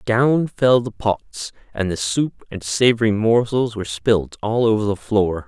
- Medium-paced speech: Yes, average, 175 wpm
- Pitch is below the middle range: Yes, low, 110 Hz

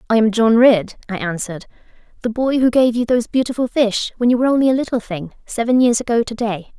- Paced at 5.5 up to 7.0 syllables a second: Yes, 6.3 syllables/s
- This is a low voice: No, high, 230 Hz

